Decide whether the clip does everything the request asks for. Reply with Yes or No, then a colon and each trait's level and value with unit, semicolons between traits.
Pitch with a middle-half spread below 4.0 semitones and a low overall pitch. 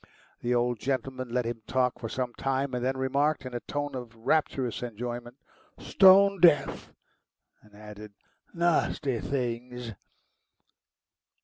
Yes: narrow, 2.5 semitones; low, 125 Hz